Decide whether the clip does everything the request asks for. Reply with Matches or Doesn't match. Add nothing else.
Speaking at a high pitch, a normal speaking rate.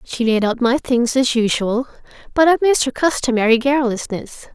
Matches